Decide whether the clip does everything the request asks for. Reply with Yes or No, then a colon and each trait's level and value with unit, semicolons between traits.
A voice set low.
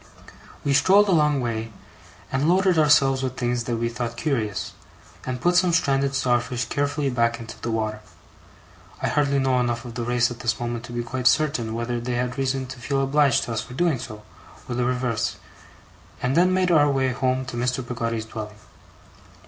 Yes: low, 125 Hz